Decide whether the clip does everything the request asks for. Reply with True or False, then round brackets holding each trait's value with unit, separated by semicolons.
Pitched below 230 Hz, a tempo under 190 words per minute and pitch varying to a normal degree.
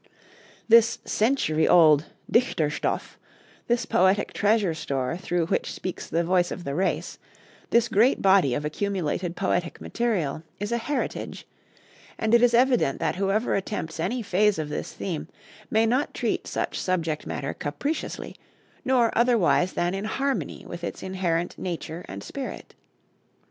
False (190 Hz; 145 wpm; 5.7 semitones)